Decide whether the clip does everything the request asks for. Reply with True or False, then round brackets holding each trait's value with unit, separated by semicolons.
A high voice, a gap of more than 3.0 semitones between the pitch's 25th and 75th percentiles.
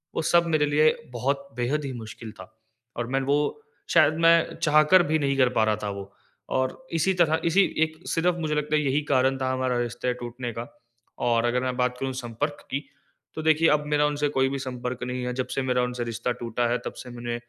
False (130 Hz; 3.5 semitones)